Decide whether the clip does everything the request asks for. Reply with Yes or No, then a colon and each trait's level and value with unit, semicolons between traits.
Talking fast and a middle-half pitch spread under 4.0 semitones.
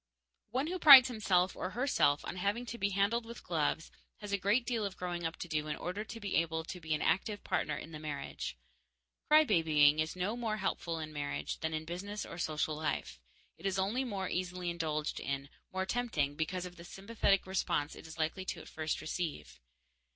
No: fast, 210 wpm; average, 4.7 semitones